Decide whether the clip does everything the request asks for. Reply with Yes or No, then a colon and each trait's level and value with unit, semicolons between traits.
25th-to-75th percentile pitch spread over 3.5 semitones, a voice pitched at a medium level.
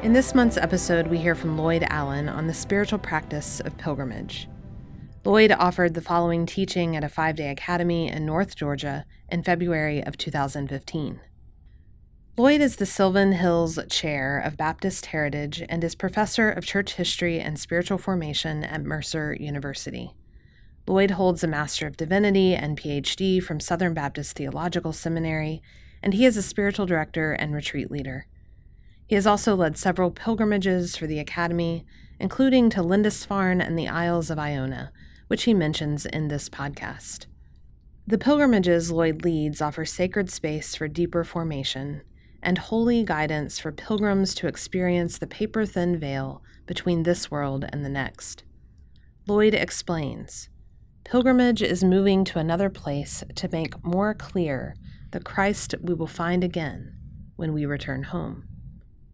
Yes: average, 4.2 semitones; medium, 170 Hz